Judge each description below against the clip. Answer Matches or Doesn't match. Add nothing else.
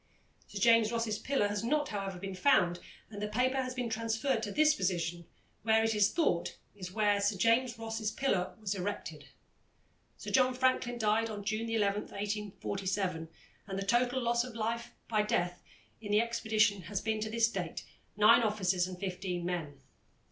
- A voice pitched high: Matches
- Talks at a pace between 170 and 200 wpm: Matches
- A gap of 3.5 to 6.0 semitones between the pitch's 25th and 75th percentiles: Doesn't match